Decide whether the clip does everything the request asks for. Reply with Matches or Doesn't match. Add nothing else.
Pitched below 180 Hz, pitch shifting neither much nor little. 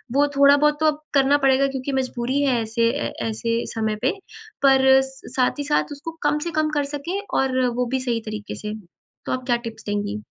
Doesn't match